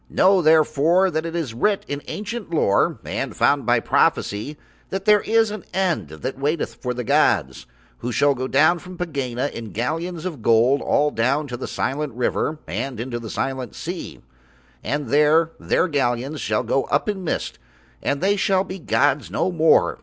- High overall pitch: No, medium, 150 Hz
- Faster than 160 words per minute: Yes, average, 175 wpm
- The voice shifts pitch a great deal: Yes, wide, 5.9 semitones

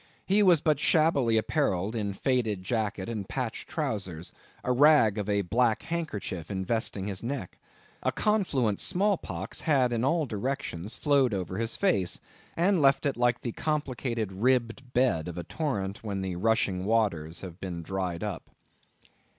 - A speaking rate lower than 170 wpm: Yes, average, 160 wpm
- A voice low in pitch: Yes, low, 115 Hz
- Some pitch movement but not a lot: No, wide, 6.1 semitones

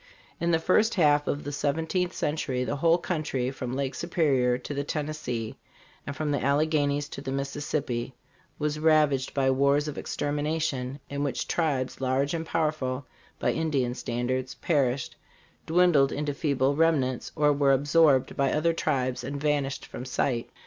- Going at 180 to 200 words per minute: No, average, 165 wpm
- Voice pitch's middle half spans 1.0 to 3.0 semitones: Yes, average, 2.7 semitones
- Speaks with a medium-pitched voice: Yes, medium, 145 Hz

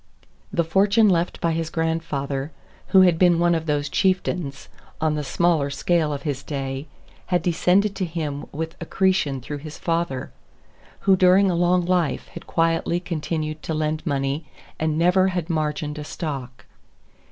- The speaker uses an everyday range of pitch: Yes, average, 3.0 semitones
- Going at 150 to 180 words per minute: Yes, average, 160 wpm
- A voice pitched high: No, medium, 165 Hz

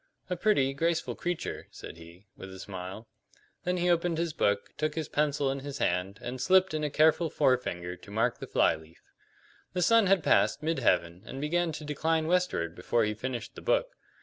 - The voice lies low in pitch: No, medium, 145 Hz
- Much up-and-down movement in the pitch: Yes, wide, 8.7 semitones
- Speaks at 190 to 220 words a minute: Yes, average, 200 wpm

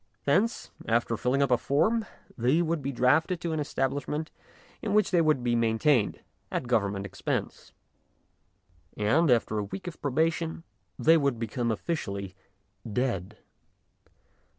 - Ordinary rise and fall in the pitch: No, wide, 5.9 semitones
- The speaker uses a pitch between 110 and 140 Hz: Yes, low, 135 Hz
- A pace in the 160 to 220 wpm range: No, slow, 135 wpm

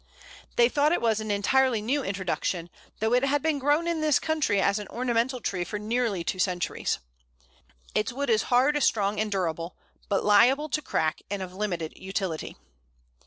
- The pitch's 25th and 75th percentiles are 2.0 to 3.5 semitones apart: No, wide, 5.4 semitones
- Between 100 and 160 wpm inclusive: No, average, 175 wpm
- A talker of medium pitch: No, high, 220 Hz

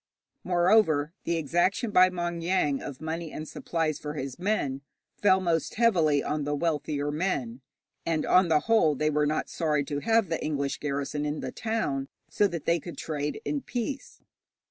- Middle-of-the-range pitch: Yes, medium, 160 Hz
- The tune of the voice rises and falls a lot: No, average, 3.7 semitones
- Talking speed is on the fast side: No, average, 175 wpm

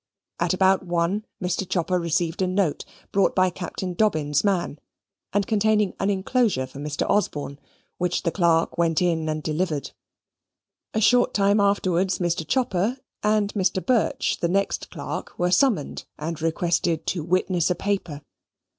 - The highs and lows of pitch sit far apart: No, average, 3.3 semitones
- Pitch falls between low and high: Yes, medium, 180 Hz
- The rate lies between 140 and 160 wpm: Yes, average, 150 wpm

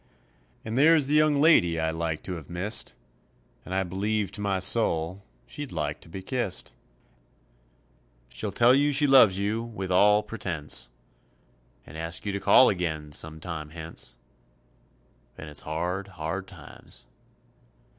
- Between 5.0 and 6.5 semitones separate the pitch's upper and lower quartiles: Yes, wide, 5.4 semitones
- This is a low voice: Yes, very low, 95 Hz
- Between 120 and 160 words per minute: Yes, average, 145 wpm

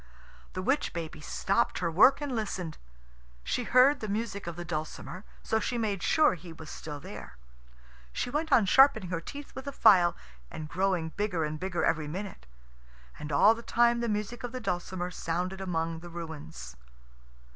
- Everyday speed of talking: Yes, average, 180 wpm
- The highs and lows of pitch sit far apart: Yes, wide, 5.9 semitones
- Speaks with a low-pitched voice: No, medium, 185 Hz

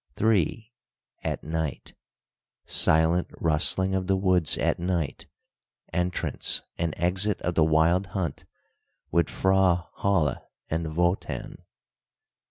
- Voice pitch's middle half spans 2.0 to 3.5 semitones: Yes, average, 2.8 semitones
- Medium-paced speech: No, slow, 105 wpm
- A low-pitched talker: Yes, very low, 90 Hz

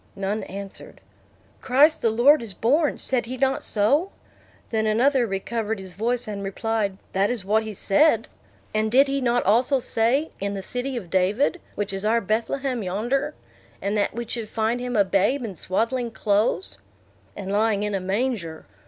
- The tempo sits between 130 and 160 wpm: No, average, 175 wpm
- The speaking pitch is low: No, high, 225 Hz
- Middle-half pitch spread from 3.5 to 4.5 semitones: Yes, average, 3.9 semitones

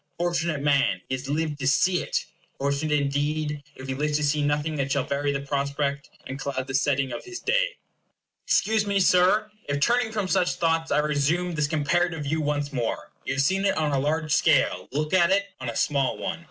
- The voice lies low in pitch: No, medium, 150 Hz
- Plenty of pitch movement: No, average, 3.6 semitones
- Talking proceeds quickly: Yes, fast, 210 wpm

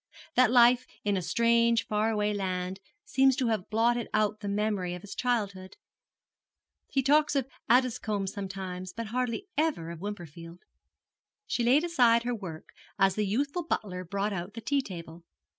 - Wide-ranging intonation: No, average, 4.4 semitones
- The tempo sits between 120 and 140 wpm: No, average, 160 wpm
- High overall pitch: Yes, high, 215 Hz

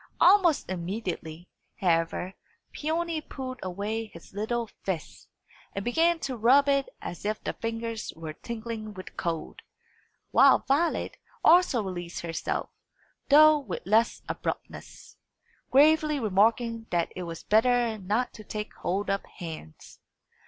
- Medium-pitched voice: No, high, 220 Hz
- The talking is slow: Yes, slow, 125 wpm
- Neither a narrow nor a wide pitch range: No, wide, 6.2 semitones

